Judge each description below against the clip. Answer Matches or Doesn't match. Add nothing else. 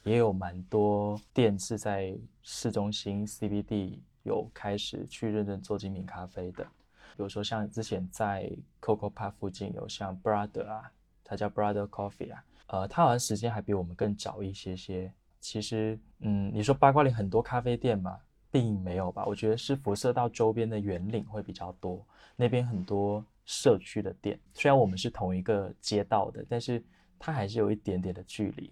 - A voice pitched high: Doesn't match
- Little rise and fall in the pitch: Matches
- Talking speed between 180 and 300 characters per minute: Doesn't match